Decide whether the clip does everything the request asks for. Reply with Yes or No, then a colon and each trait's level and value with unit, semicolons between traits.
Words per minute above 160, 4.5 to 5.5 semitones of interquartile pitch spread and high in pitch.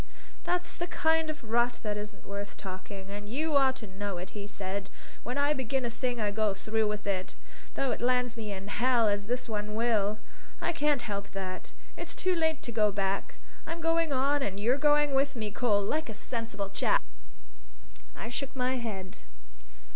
Yes: average, 190 wpm; average, 5.0 semitones; high, 230 Hz